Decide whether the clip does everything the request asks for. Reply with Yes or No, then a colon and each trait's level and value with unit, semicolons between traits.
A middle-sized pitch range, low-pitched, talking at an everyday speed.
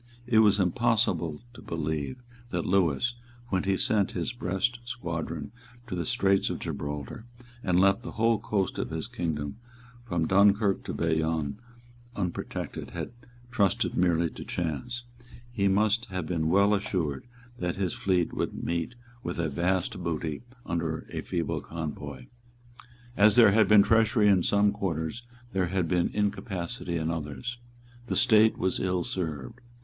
Yes: average, 4.1 semitones; very low, 95 Hz; average, 150 wpm